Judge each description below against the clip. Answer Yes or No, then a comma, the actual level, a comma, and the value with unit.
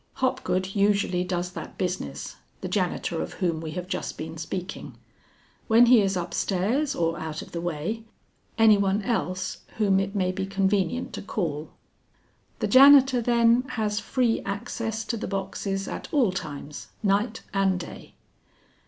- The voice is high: Yes, high, 195 Hz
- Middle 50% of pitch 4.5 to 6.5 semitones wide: No, average, 3.9 semitones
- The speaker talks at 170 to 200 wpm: No, average, 155 wpm